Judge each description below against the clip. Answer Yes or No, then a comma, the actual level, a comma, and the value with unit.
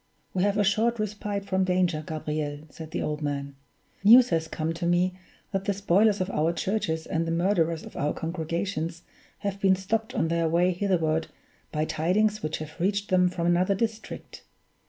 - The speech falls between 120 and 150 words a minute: No, average, 180 wpm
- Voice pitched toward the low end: No, medium, 180 Hz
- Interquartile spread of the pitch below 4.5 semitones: Yes, average, 3.8 semitones